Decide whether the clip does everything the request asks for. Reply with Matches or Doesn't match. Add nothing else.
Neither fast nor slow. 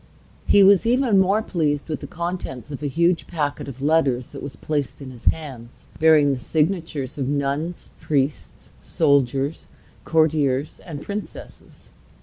Matches